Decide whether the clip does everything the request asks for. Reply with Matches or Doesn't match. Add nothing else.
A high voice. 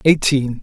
Doesn't match